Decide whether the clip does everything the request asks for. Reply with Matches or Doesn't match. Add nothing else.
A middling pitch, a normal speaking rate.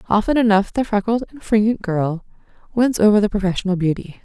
Doesn't match